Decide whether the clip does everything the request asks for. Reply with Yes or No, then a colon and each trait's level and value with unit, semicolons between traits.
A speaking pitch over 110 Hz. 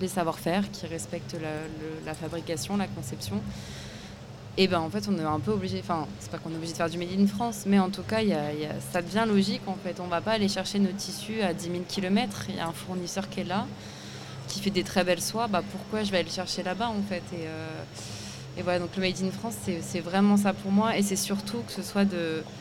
Yes: medium, 185 Hz